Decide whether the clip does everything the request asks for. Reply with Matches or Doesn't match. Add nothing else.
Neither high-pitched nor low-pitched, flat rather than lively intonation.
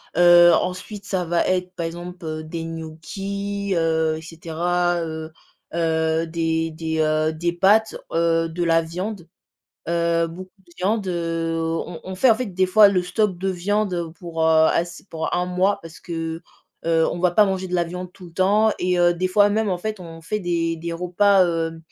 Matches